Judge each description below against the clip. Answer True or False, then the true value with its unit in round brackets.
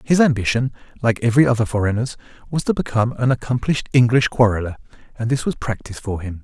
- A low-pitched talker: True (120 Hz)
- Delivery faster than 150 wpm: True (175 wpm)